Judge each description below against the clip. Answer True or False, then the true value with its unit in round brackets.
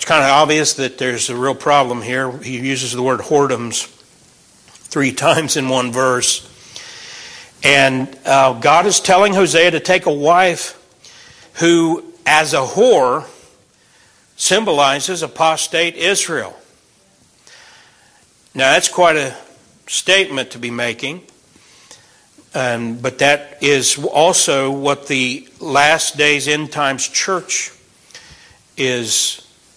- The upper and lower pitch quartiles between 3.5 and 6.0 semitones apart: True (4.0 semitones)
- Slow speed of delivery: True (115 wpm)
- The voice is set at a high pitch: False (140 Hz)